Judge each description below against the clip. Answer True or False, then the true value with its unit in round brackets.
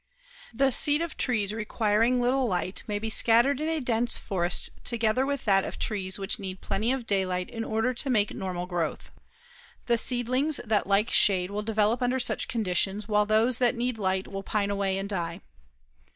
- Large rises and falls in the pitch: False (3.8 semitones)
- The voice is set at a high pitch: True (215 Hz)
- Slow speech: False (185 wpm)